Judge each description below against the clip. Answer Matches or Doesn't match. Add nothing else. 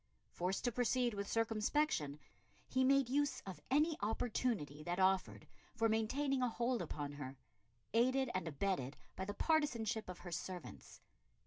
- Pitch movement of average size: Doesn't match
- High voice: Matches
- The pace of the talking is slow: Doesn't match